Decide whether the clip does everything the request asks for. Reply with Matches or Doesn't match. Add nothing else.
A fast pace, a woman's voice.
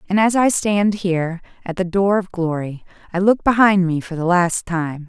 Matches